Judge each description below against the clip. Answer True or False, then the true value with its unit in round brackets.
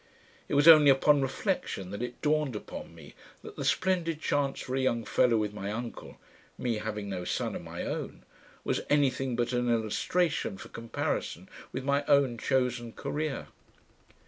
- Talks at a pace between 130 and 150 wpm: False (170 wpm)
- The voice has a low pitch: True (125 Hz)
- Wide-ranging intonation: False (4.2 semitones)